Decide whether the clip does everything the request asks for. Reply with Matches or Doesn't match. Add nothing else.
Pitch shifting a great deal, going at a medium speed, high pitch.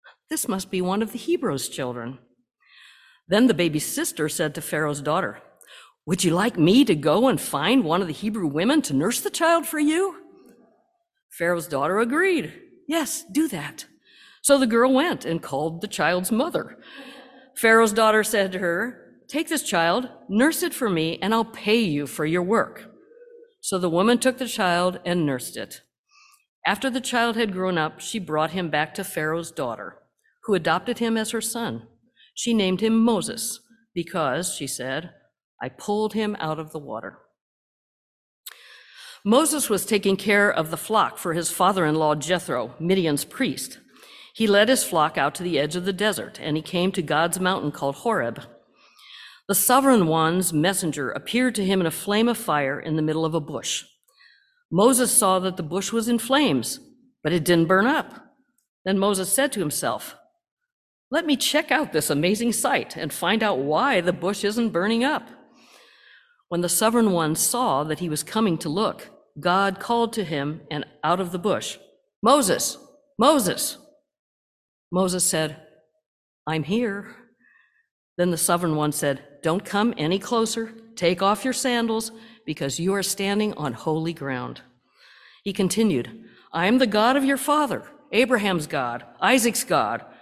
Matches